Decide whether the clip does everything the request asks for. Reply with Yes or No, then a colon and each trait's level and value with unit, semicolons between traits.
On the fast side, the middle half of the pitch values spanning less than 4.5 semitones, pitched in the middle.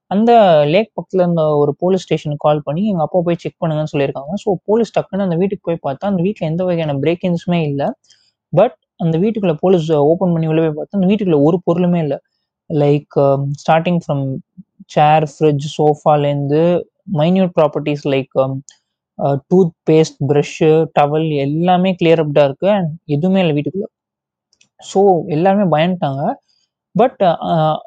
Yes: fast, 145 wpm; average, 3.8 semitones; medium, 160 Hz